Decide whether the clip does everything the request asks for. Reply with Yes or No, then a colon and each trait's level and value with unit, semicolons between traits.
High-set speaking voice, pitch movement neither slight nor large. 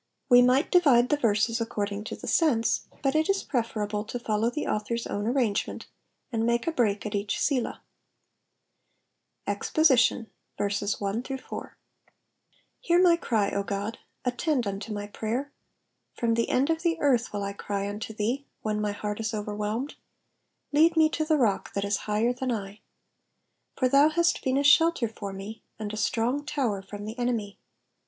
Yes: high, 230 Hz; average, 4.7 semitones